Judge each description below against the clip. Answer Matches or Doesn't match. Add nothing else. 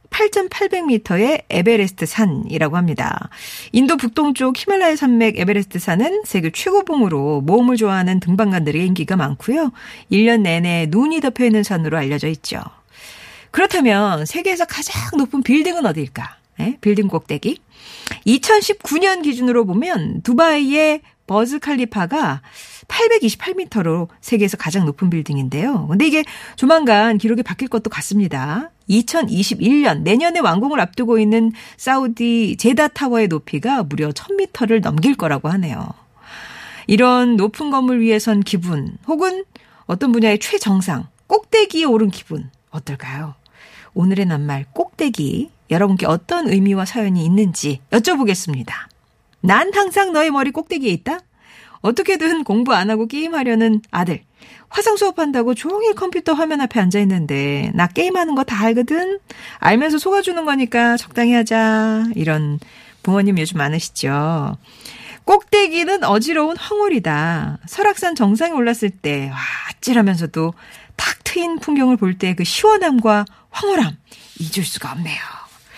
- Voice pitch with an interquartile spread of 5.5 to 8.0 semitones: Doesn't match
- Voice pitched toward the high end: Matches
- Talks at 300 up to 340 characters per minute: Matches